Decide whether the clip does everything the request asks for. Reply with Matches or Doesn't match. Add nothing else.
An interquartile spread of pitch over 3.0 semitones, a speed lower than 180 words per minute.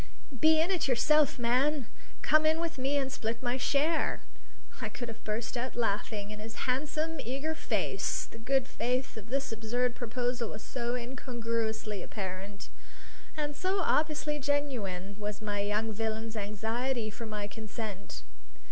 Matches